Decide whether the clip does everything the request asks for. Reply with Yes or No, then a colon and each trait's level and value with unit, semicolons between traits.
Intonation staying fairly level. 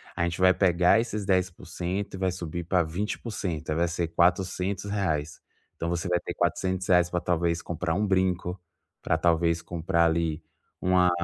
Yes: narrow, 1.8 semitones